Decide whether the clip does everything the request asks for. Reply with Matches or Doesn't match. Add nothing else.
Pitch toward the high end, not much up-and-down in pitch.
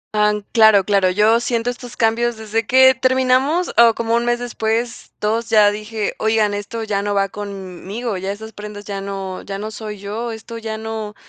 Matches